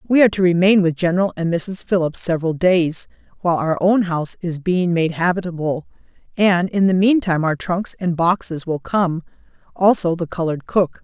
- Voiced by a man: No, female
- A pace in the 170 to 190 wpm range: Yes, average, 180 wpm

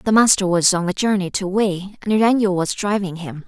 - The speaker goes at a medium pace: No, fast, 240 wpm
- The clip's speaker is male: No, female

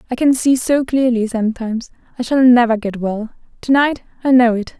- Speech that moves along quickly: No, average, 190 wpm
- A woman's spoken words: Yes, female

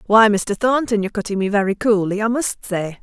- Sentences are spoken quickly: Yes, fast, 220 wpm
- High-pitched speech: Yes, high, 210 Hz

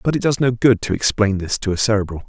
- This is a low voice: Yes, low, 110 Hz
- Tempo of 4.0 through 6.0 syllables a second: No, 6.5 syllables/s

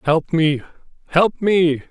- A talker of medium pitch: Yes, medium, 165 Hz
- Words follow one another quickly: No, slow, 125 wpm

